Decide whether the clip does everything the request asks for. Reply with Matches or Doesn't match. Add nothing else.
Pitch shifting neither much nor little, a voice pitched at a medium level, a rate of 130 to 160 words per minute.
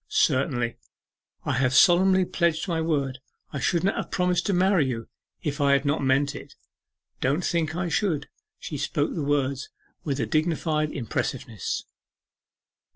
Matches